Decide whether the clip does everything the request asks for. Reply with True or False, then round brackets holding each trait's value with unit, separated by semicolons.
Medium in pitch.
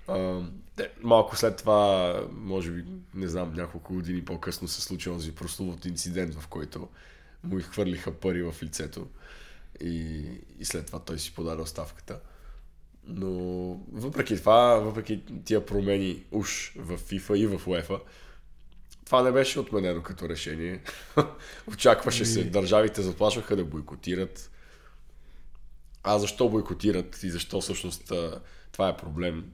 False (90 Hz)